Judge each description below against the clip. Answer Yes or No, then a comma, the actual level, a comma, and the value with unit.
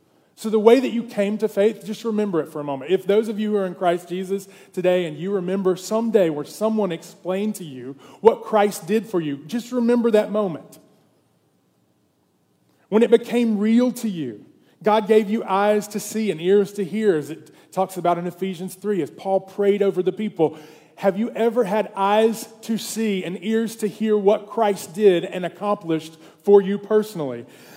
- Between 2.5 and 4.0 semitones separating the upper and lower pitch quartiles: Yes, average, 3.3 semitones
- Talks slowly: No, average, 195 wpm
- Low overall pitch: No, high, 200 Hz